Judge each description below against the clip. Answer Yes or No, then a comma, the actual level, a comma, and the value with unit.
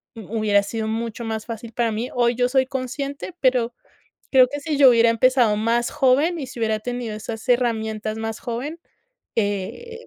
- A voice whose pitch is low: No, high, 235 Hz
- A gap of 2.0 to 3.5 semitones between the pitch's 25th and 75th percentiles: Yes, average, 2.7 semitones